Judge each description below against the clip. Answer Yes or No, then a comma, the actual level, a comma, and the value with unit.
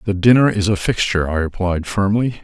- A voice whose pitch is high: No, low, 100 Hz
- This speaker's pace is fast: No, average, 195 wpm